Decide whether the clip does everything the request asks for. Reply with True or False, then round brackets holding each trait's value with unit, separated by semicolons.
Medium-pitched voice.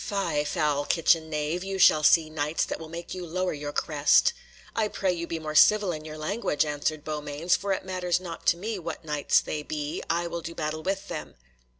True (165 Hz)